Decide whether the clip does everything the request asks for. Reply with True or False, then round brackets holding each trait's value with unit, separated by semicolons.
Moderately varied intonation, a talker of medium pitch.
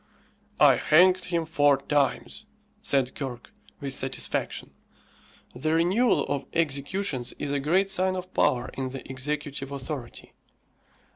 True (4.2 semitones; 145 Hz)